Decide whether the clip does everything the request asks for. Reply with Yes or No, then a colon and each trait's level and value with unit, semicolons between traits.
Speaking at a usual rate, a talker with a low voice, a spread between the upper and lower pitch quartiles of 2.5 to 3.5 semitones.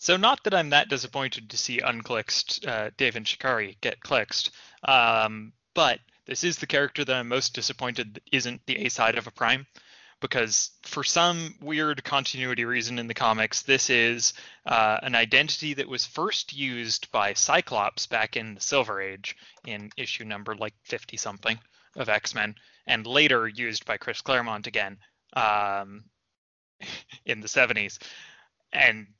No: average, 160 wpm; low, 120 Hz; average, 4.1 semitones